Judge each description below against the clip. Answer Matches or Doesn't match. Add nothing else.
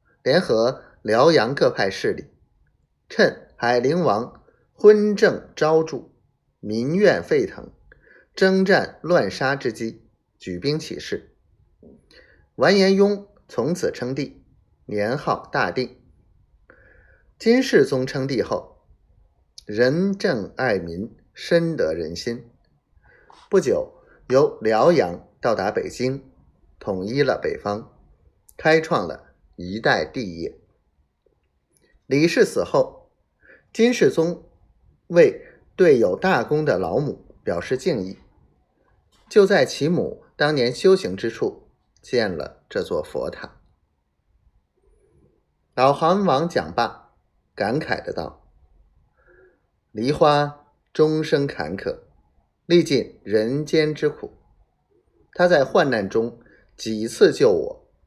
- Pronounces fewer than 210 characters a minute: Matches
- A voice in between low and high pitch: Matches